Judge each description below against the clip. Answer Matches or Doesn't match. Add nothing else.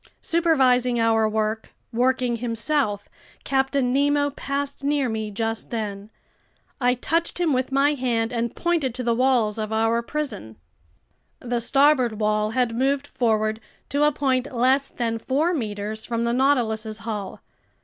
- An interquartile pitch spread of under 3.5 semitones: Doesn't match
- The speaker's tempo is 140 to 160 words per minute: Matches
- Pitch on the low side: Doesn't match